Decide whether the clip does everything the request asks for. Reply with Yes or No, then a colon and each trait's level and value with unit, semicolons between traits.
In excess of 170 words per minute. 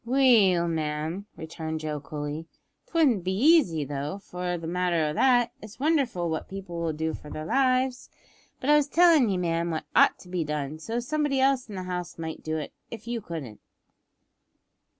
Yes: average, 190 wpm